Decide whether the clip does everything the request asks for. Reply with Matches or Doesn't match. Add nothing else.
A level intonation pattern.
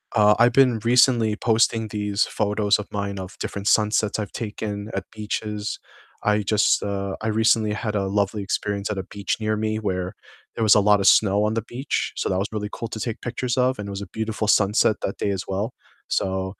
Matches